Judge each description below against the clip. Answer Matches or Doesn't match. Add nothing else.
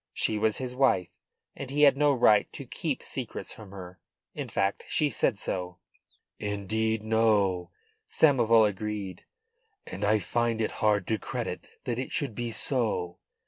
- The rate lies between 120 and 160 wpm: Matches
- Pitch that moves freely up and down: Doesn't match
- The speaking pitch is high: Doesn't match